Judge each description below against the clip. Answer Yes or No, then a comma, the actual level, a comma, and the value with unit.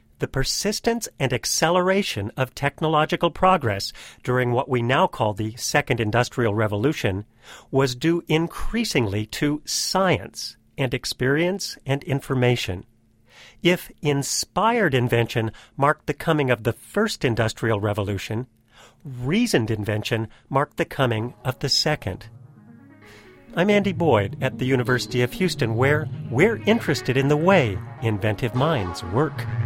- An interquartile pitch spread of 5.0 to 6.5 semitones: Yes, average, 5.3 semitones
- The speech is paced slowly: Yes, slow, 125 wpm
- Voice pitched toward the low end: Yes, low, 130 Hz